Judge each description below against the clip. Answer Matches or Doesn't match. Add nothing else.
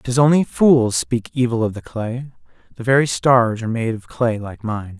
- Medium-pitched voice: Doesn't match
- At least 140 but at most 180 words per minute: Doesn't match